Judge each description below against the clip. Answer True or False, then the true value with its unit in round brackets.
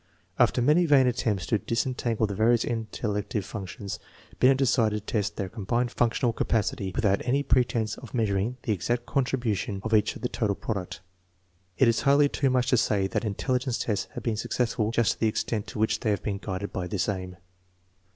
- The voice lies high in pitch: False (110 Hz)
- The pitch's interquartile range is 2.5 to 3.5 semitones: True (3.2 semitones)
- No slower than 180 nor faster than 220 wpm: True (195 wpm)